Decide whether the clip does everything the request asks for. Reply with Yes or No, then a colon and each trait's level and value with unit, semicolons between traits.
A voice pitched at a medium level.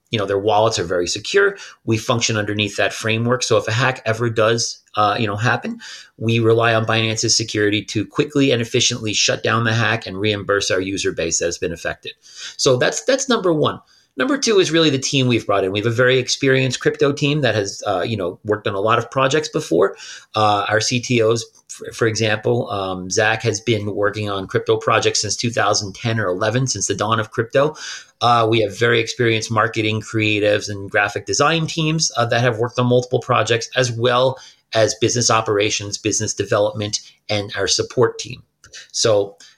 No: low, 115 Hz